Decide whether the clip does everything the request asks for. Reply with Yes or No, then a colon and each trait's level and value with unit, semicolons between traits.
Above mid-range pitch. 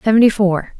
Yes: high, 205 Hz